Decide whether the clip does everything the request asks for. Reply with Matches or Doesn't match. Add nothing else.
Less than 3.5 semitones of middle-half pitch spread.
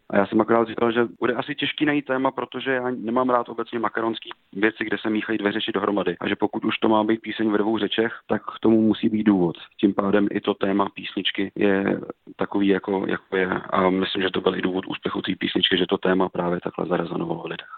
Matches